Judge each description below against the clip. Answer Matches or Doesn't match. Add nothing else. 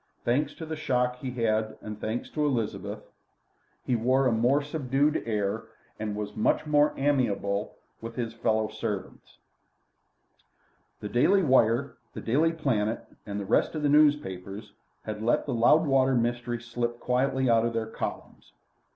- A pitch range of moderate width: Matches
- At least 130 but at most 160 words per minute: Matches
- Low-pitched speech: Matches